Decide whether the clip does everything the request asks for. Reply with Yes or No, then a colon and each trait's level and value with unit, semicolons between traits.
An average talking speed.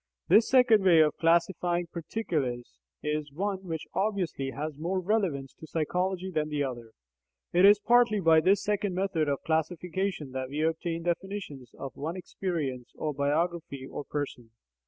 Yes: average, 155 wpm